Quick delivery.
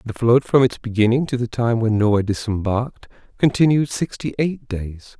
No: average, 175 wpm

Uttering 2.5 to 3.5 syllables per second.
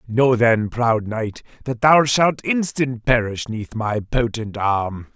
Yes: 3.4 syllables/s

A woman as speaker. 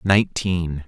No: male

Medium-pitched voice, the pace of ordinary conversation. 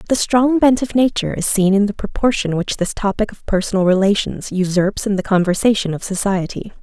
No: high, 200 Hz; average, 195 wpm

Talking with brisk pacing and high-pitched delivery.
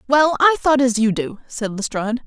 Yes: fast, 210 wpm; very high, 250 Hz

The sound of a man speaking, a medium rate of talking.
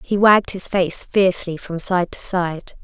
No: female; average, 190 wpm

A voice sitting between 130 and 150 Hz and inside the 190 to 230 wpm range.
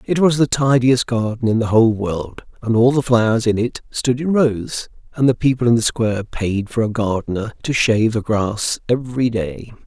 No: low, 115 Hz; fast, 205 wpm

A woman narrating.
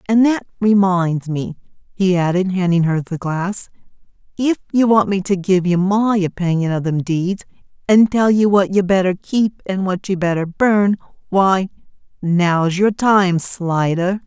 Yes: female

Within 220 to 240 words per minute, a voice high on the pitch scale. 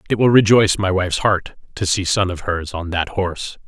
No: fast, 230 wpm; very low, 95 Hz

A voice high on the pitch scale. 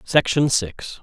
No: low, 125 Hz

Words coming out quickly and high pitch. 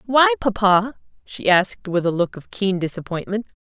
No: average, 165 wpm; high, 205 Hz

